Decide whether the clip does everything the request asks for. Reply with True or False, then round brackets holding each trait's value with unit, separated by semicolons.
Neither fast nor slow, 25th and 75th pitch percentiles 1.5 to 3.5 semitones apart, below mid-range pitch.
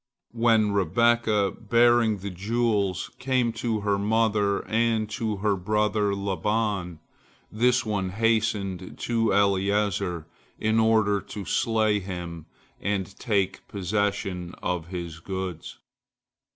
False (110 wpm; 2.8 semitones; 105 Hz)